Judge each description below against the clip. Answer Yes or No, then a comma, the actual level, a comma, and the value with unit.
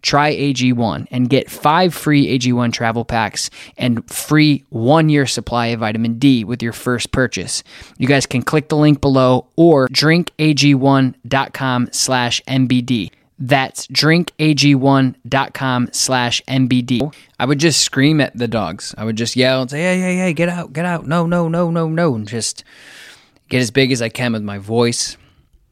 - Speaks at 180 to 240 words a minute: No, average, 155 wpm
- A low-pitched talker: Yes, low, 130 Hz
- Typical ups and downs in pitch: Yes, average, 3.5 semitones